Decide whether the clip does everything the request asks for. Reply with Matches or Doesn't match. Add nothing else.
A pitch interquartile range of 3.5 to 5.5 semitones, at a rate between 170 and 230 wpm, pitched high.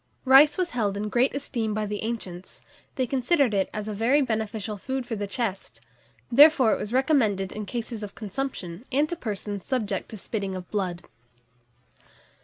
Matches